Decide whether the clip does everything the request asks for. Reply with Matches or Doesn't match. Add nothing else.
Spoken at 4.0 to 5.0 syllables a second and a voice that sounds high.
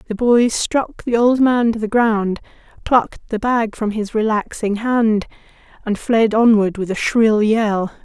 Matches